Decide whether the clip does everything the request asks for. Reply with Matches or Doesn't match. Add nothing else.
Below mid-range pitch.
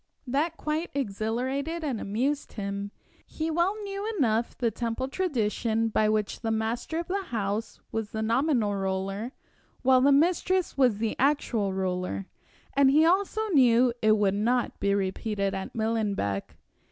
Doesn't match